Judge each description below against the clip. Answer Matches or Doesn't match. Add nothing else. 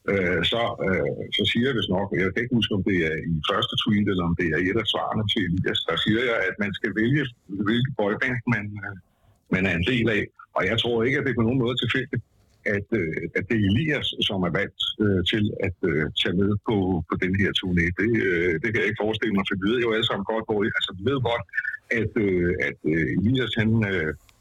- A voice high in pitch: Doesn't match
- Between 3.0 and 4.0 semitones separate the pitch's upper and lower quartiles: Matches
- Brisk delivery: Matches